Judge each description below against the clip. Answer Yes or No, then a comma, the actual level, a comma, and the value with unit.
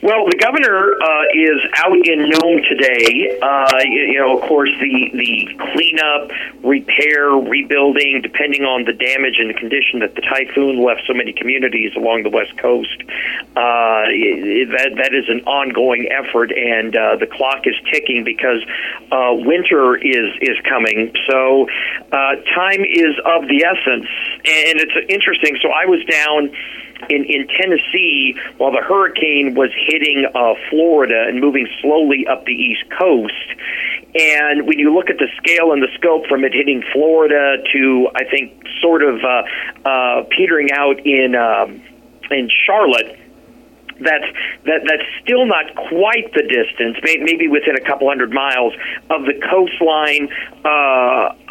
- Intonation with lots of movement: No, average, 3.7 semitones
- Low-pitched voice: No, medium, 150 Hz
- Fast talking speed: No, average, 155 wpm